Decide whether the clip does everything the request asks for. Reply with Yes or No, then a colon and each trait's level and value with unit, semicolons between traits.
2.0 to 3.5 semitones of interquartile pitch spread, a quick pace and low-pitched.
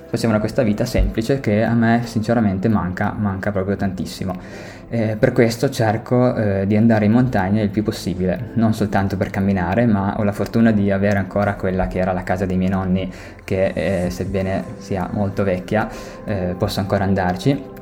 Yes: average, 2.7 semitones; fast, 180 wpm; low, 100 Hz